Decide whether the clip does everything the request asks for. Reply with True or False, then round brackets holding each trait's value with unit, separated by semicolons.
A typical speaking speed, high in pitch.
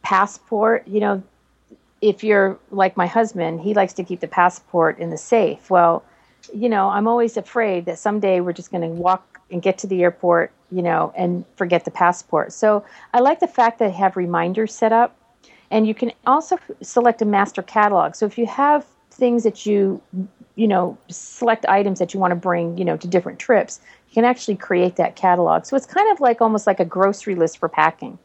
False (210 wpm; 195 Hz)